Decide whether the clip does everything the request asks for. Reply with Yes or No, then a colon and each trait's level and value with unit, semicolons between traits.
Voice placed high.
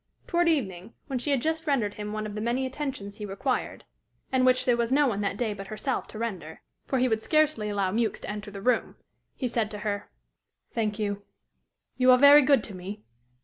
Yes: high, 230 Hz